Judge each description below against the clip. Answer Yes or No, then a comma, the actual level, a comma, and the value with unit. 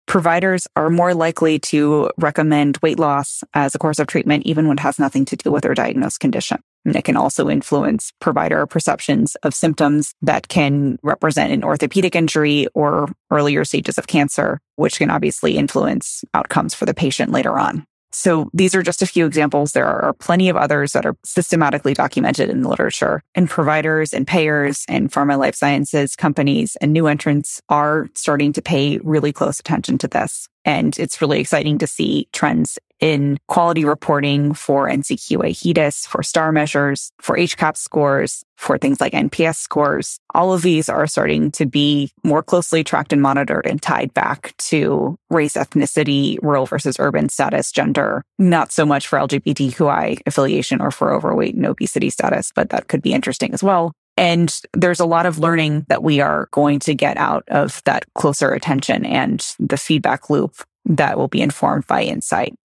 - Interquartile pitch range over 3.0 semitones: No, narrow, 2.5 semitones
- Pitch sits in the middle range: Yes, medium, 150 Hz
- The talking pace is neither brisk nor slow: Yes, average, 180 wpm